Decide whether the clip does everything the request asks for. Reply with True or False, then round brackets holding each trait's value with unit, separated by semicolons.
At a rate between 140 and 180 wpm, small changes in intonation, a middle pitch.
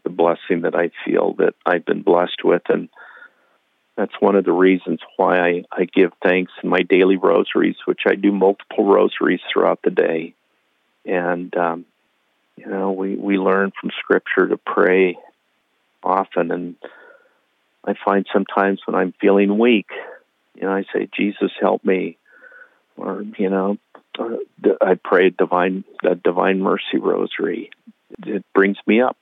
False (155 wpm; 1.6 semitones; 95 Hz)